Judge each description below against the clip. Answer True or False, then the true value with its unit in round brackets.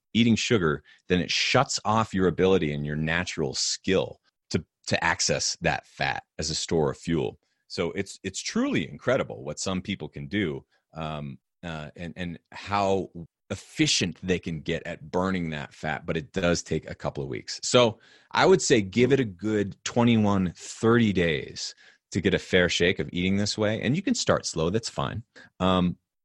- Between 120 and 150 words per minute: False (185 wpm)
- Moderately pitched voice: False (90 Hz)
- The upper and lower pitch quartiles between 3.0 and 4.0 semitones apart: True (3.6 semitones)